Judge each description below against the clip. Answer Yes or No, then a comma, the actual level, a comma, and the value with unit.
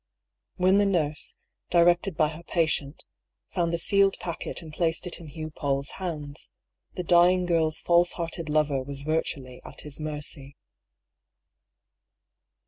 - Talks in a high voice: No, medium, 160 Hz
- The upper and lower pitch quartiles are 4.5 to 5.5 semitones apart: No, average, 2.8 semitones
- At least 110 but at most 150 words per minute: Yes, slow, 135 wpm